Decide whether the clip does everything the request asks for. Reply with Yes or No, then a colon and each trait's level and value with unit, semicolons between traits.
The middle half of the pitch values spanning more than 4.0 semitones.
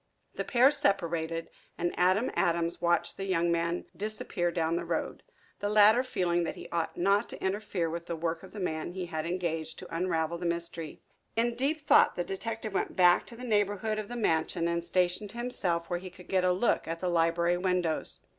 No: average, 3.3 semitones